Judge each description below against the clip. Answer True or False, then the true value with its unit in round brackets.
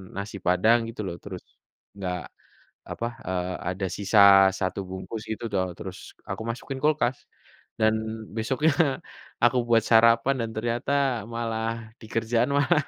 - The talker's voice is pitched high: False (115 Hz)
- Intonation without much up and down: False (3.0 semitones)